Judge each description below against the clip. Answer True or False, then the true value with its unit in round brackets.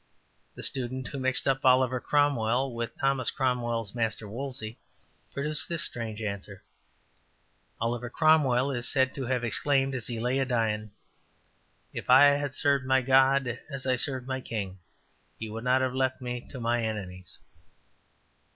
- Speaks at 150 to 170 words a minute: True (160 wpm)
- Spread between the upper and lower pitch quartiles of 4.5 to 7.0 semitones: False (2.6 semitones)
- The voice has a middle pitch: False (130 Hz)